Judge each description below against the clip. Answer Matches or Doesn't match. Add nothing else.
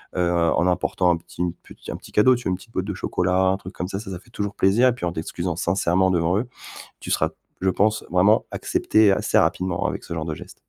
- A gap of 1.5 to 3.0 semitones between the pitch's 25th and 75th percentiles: Matches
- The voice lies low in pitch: Matches